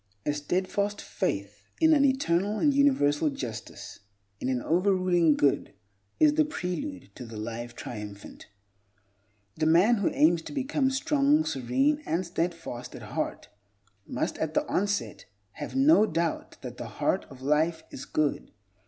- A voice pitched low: No, medium, 175 Hz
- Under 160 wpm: Yes, average, 150 wpm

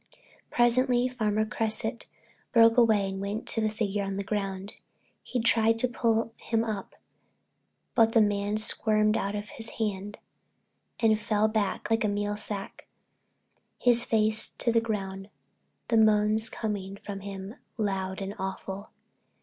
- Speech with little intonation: Yes, narrow, 2.0 semitones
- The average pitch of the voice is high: Yes, high, 215 Hz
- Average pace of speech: Yes, average, 145 wpm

